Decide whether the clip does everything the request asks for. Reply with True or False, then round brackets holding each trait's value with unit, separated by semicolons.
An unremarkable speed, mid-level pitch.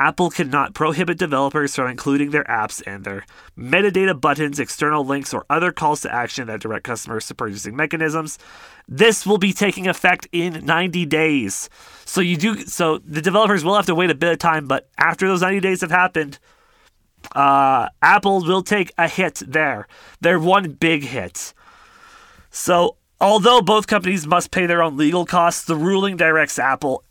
True (175 wpm; 170 Hz)